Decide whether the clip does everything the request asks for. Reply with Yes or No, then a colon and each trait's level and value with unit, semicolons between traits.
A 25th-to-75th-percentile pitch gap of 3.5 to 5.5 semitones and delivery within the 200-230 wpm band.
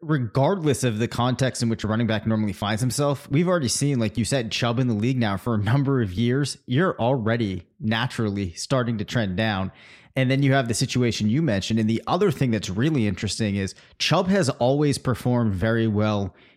Yes: average, 3.8 semitones; fast, 205 wpm